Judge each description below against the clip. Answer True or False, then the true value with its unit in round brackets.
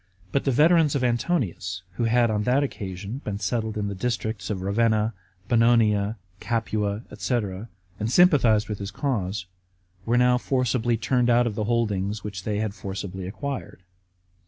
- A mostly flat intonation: False (3.4 semitones)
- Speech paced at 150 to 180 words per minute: True (160 wpm)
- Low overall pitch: True (110 Hz)